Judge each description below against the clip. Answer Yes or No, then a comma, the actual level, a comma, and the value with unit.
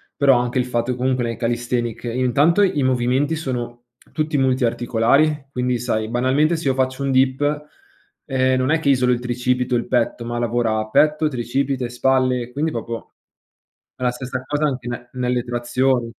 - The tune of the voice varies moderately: No, narrow, 2.1 semitones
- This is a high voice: No, low, 125 Hz